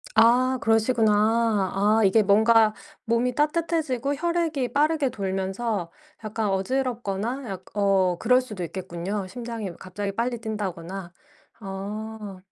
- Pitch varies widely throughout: No, average, 4.2 semitones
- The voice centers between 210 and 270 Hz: Yes, high, 220 Hz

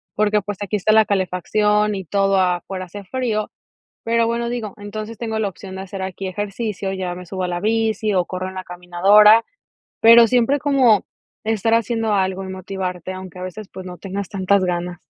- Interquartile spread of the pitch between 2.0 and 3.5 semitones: Yes, average, 2.7 semitones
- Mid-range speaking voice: No, high, 200 Hz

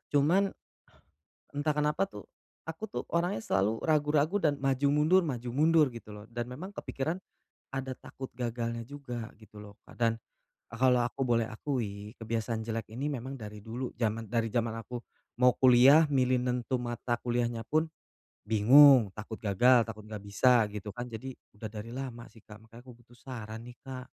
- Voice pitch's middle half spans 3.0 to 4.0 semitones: Yes, average, 3.3 semitones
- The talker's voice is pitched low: Yes, low, 120 Hz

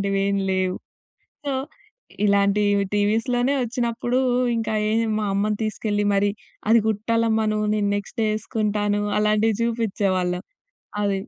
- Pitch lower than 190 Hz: No, high, 210 Hz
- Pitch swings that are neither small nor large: No, narrow, 2.0 semitones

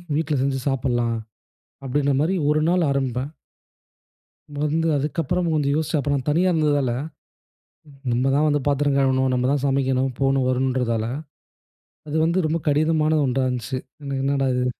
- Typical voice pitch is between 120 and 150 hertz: Yes, medium, 140 Hz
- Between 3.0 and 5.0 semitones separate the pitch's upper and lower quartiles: No, narrow, 2.6 semitones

